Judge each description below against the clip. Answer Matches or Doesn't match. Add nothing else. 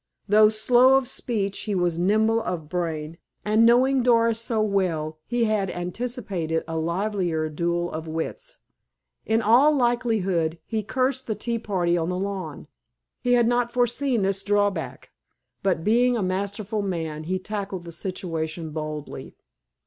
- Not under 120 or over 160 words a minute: Matches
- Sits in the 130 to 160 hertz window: Doesn't match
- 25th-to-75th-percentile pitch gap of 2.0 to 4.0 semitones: Doesn't match